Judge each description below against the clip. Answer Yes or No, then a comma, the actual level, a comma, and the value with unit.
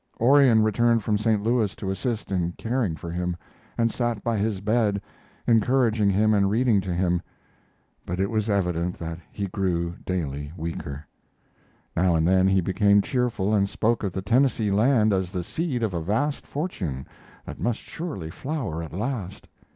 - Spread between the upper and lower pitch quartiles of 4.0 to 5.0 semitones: Yes, average, 4.5 semitones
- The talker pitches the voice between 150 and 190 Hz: No, low, 100 Hz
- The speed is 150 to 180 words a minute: Yes, average, 170 wpm